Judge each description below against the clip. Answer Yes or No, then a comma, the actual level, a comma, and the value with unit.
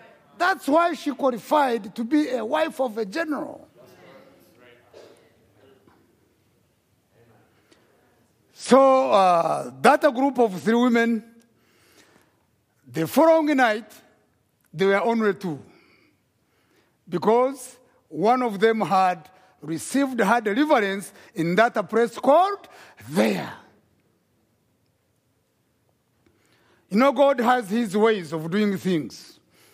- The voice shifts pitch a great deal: Yes, wide, 5.8 semitones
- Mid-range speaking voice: No, high, 230 Hz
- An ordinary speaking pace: No, slow, 95 wpm